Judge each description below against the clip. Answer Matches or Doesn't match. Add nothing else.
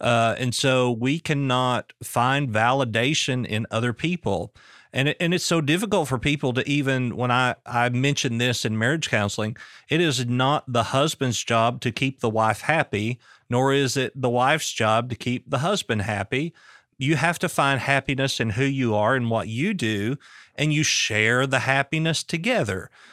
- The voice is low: Matches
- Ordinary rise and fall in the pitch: Matches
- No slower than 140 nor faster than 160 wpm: Doesn't match